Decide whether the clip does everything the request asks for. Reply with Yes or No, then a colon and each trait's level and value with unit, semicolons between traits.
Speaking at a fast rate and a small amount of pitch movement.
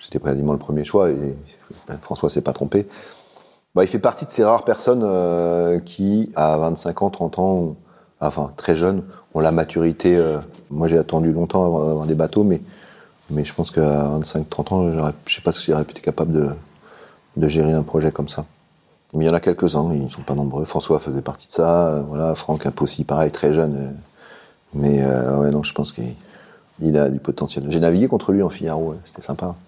Yes: fast, 225 wpm; narrow, 2.3 semitones